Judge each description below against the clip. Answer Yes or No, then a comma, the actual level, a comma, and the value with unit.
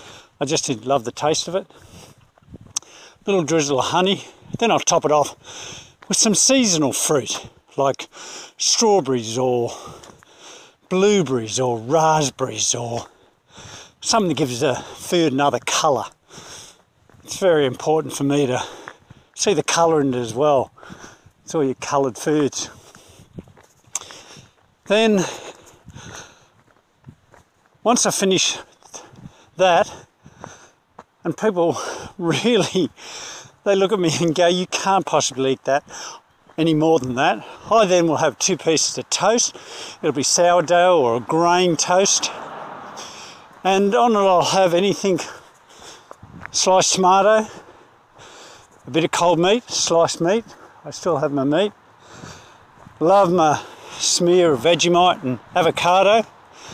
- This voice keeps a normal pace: No, slow, 125 wpm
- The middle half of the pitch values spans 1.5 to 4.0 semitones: No, average, 5.0 semitones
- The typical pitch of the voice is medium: Yes, medium, 165 Hz